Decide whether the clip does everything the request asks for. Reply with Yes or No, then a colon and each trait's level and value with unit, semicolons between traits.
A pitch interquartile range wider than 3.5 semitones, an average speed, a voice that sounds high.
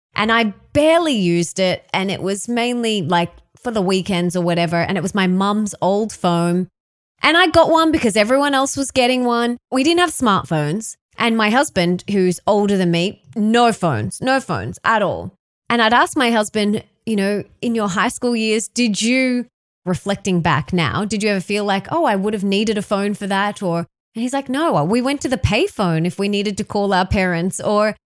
No: average, 4.3 semitones; fast, 210 wpm; high, 210 Hz